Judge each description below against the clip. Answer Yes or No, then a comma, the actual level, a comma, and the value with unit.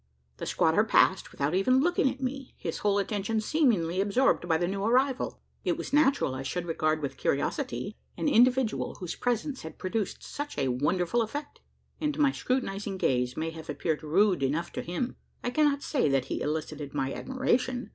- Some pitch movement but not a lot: No, wide, 8.3 semitones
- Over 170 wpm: Yes, average, 180 wpm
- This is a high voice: Yes, high, 200 Hz